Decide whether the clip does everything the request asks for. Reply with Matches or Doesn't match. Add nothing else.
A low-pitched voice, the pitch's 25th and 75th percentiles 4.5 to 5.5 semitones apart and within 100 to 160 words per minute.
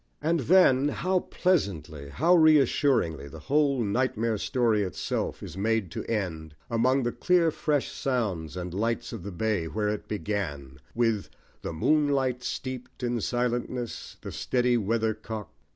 Matches